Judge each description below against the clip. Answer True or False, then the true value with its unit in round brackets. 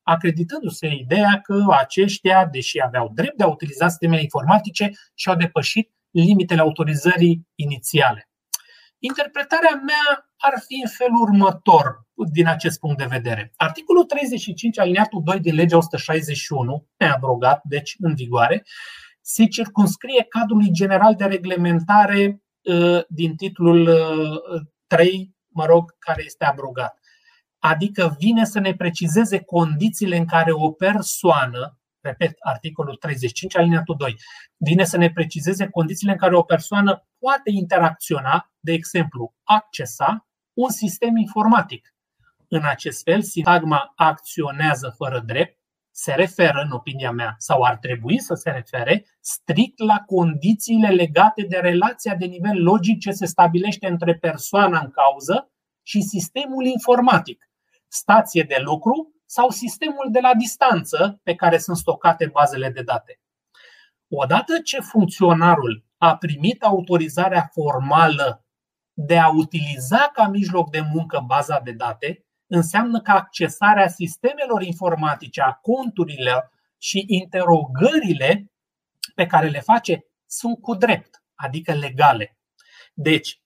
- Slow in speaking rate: False (125 wpm)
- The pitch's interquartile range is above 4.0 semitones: True (4.7 semitones)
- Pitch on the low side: False (175 Hz)